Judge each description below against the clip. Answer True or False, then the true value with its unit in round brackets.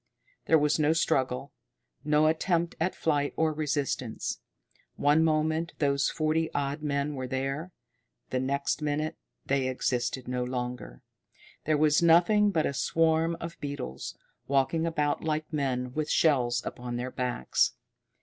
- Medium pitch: True (145 Hz)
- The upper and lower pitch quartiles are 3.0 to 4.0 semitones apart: True (3.4 semitones)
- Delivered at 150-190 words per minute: False (140 wpm)